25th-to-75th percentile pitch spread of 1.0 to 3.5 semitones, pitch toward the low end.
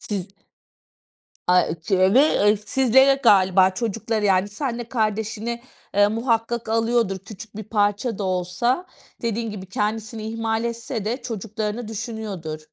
No: average, 2.7 semitones; high, 220 Hz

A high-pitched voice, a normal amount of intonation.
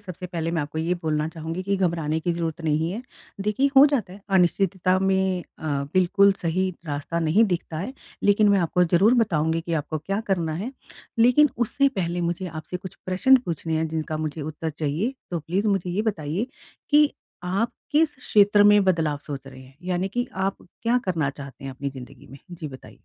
No: medium, 175 Hz; average, 4.1 semitones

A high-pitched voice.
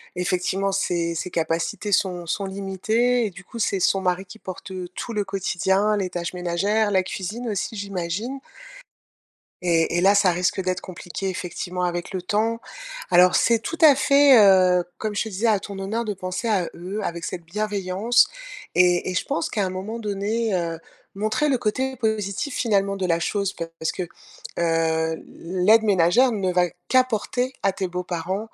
Yes: high, 195 Hz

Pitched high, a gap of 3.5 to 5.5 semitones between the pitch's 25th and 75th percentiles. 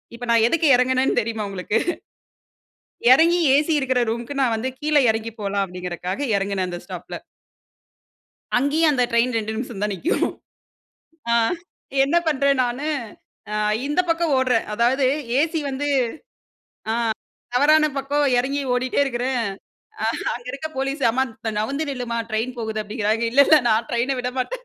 Yes: very high, 250 Hz; average, 4.0 semitones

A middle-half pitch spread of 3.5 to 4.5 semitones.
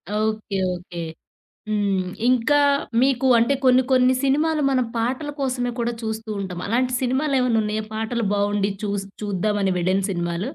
Yes: average, 4.1 semitones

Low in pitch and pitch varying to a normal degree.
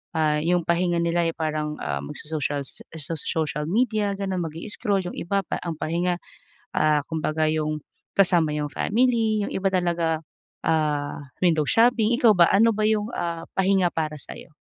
No: medium, 170 Hz; average, 4.2 semitones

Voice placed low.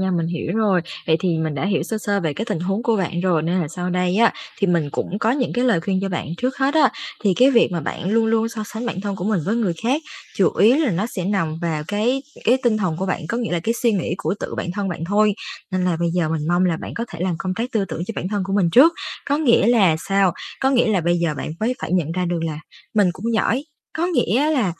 No: high, 195 Hz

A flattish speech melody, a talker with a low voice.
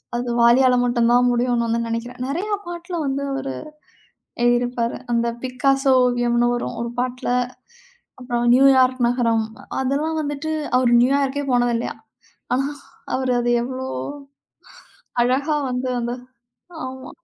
No: narrow, 2.0 semitones; very high, 250 Hz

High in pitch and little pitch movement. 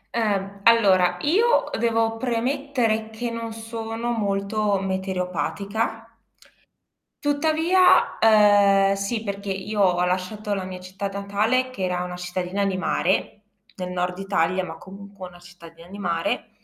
No: high, 200 Hz; average, 3.4 semitones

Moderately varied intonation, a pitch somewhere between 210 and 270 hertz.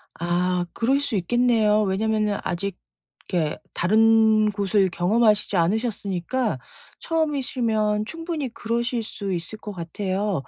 Yes: average, 3.6 semitones; high, 215 Hz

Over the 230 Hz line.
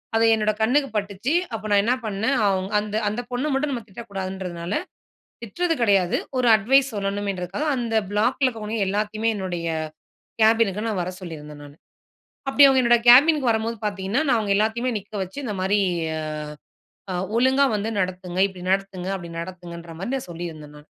No: high, 205 Hz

